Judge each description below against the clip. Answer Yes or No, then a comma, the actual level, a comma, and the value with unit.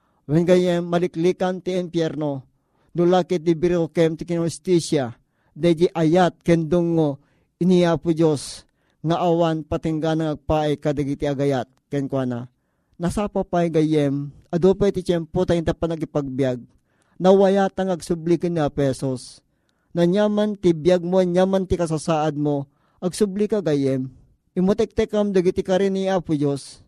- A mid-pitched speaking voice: Yes, medium, 170 Hz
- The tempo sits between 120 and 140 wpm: Yes, average, 130 wpm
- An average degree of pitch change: Yes, average, 3.8 semitones